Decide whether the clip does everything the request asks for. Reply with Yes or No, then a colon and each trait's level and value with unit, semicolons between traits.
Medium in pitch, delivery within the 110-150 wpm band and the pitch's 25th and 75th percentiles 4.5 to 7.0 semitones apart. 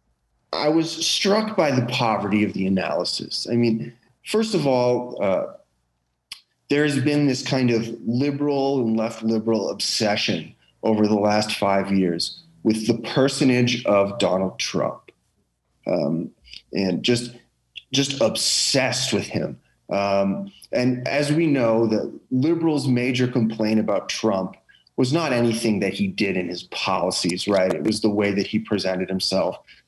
No: low, 115 Hz; average, 145 wpm; average, 4.9 semitones